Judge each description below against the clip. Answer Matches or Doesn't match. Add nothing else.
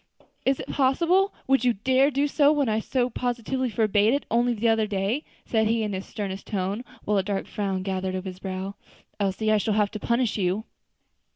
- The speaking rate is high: Matches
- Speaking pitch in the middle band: Doesn't match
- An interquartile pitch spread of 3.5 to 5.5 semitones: Matches